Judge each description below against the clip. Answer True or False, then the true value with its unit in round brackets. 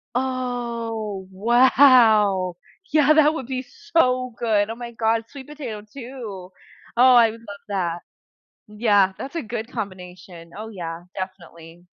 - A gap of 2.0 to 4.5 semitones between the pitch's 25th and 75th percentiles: False (4.9 semitones)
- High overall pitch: True (225 Hz)